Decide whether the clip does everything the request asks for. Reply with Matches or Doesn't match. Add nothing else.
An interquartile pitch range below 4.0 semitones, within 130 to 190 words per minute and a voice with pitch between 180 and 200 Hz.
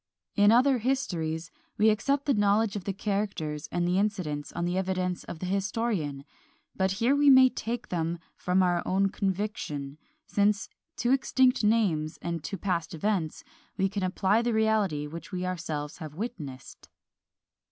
Doesn't match